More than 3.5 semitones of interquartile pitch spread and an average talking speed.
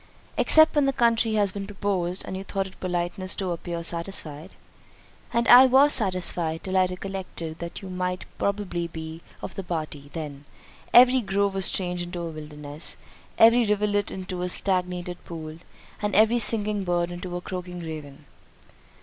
No: average, 3.1 semitones; average, 160 wpm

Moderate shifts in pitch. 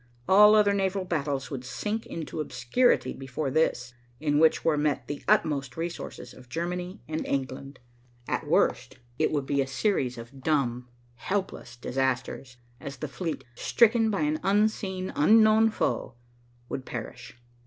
No: wide, 6.4 semitones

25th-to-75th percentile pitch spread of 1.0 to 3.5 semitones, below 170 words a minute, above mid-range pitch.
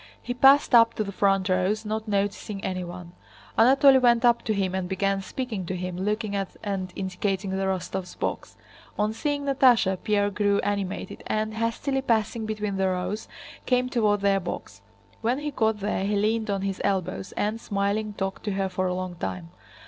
No: average, 2.7 semitones; average, 185 wpm; high, 205 Hz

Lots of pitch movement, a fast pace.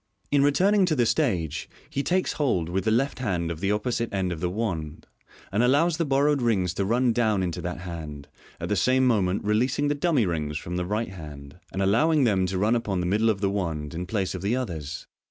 Yes: wide, 6.4 semitones; fast, 230 wpm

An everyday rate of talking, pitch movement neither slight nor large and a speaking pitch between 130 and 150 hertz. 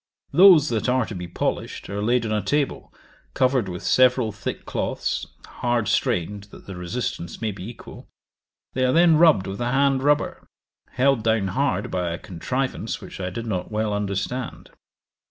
No: average, 170 wpm; average, 4.9 semitones; low, 115 Hz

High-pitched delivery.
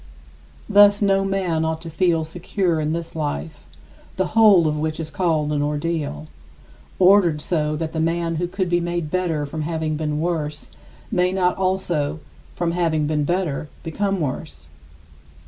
No: medium, 165 Hz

